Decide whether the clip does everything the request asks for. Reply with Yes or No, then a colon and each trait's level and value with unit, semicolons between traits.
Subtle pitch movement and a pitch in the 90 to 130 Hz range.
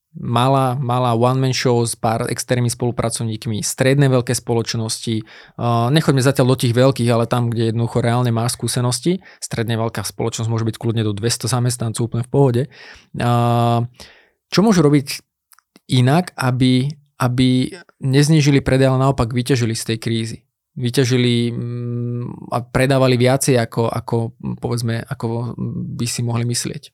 Yes: narrow, 2.1 semitones; low, 120 Hz